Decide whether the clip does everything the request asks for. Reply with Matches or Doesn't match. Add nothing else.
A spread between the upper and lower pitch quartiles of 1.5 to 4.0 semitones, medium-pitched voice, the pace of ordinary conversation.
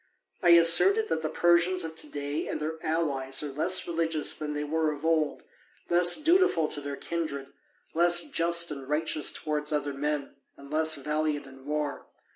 Matches